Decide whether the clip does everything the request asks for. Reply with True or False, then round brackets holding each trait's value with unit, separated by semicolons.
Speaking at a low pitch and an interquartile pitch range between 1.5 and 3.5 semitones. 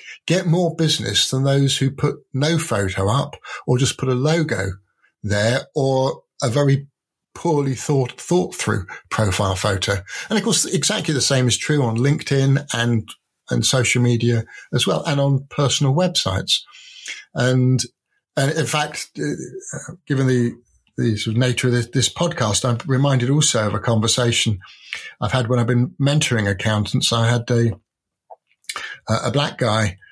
False (130 Hz; 4.0 semitones)